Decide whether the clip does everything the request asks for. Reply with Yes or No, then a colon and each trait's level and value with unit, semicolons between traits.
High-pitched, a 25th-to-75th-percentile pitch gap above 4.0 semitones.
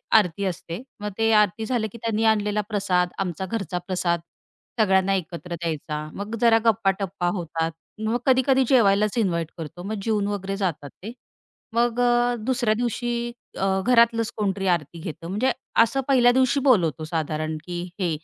Yes: high, 200 Hz; average, 4.7 semitones